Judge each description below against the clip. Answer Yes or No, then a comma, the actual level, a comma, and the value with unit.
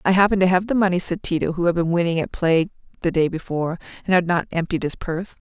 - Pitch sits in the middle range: Yes, medium, 175 Hz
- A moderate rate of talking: No, fast, 250 wpm